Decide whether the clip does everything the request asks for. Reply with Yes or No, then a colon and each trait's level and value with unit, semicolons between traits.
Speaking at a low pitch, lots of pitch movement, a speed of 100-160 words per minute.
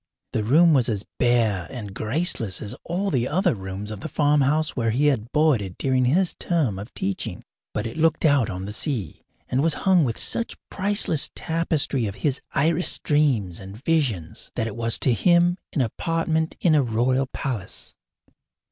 No: low, 130 Hz; wide, 6.6 semitones; average, 175 wpm